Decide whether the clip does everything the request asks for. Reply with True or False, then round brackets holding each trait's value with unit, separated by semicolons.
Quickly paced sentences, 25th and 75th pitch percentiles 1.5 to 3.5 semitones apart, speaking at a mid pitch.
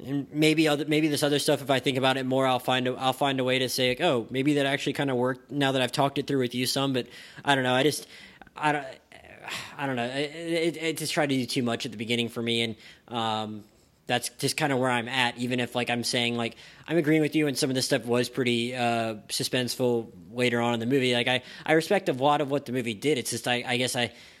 False (280 wpm; 3.1 semitones; 130 Hz)